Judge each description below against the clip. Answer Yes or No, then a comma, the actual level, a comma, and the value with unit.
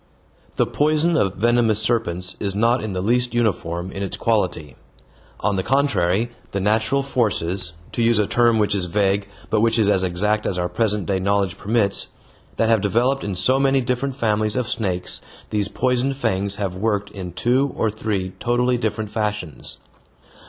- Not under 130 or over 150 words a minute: No, average, 175 wpm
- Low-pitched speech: Yes, low, 105 Hz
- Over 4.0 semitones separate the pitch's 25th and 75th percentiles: No, average, 3.6 semitones